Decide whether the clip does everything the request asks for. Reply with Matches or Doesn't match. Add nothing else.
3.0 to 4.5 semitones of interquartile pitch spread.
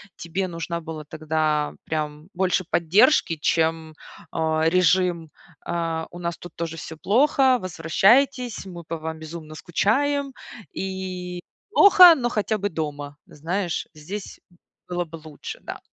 Matches